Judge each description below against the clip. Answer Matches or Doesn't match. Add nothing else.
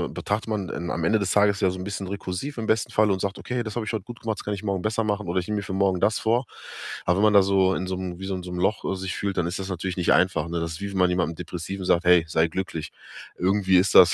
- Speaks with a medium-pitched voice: Doesn't match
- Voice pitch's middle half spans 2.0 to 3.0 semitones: Matches